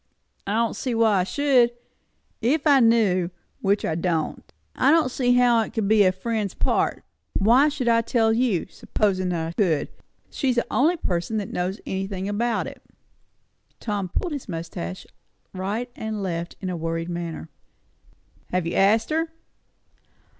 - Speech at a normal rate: Yes, average, 160 wpm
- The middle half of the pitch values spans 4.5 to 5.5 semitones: Yes, average, 4.8 semitones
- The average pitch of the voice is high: Yes, high, 210 Hz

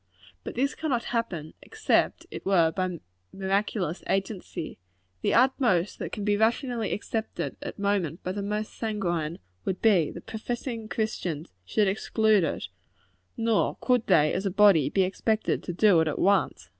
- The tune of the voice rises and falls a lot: No, average, 3.9 semitones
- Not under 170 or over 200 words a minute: No, average, 155 wpm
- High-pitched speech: Yes, high, 200 Hz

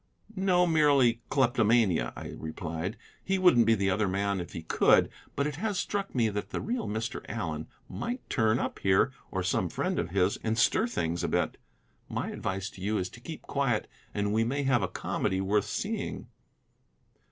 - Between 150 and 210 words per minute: Yes, average, 185 wpm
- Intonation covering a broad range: Yes, wide, 6.6 semitones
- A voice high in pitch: No, low, 110 Hz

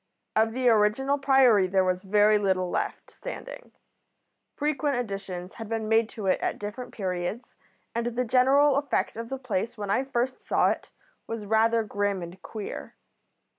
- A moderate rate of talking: Yes, average, 165 wpm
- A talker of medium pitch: No, high, 225 Hz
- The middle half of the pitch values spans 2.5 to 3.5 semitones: No, average, 4.1 semitones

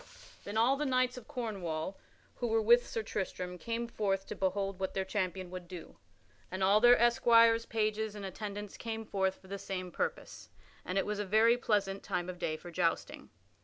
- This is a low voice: No, high, 205 Hz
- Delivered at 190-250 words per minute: Yes, average, 195 wpm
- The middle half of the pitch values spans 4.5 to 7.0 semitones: No, average, 3.3 semitones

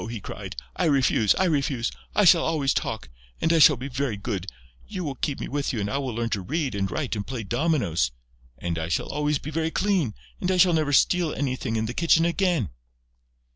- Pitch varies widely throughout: Yes, wide, 6.4 semitones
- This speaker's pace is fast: Yes, fast, 220 wpm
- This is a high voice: No, medium, 140 Hz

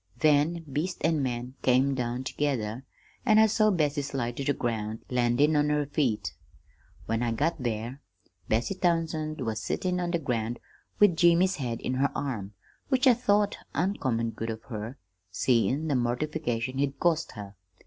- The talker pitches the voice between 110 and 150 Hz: Yes, low, 135 Hz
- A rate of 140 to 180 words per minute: Yes, average, 165 wpm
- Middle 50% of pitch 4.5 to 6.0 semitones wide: Yes, average, 5.3 semitones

